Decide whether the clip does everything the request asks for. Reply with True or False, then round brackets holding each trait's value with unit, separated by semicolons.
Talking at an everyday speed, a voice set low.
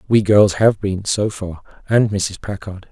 True (185 wpm; 100 Hz)